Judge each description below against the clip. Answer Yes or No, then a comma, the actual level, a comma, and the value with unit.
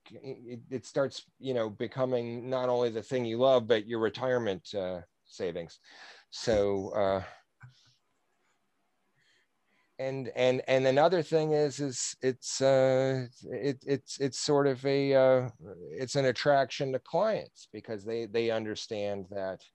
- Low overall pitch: Yes, low, 130 Hz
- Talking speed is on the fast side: No, slow, 135 wpm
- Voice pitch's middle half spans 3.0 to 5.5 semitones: No, narrow, 2.6 semitones